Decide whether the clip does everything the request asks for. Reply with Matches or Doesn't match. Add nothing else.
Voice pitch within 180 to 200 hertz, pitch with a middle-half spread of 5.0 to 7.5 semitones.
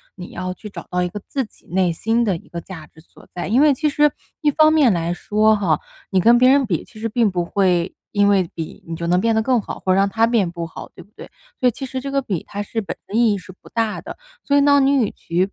Doesn't match